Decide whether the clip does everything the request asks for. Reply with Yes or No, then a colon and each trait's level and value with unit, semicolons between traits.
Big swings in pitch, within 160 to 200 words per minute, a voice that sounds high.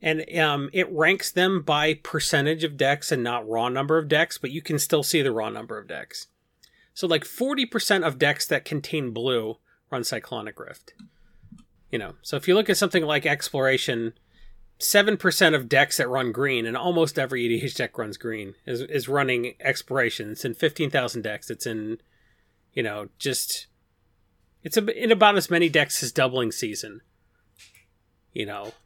No: wide, 6.5 semitones; average, 175 wpm; medium, 145 Hz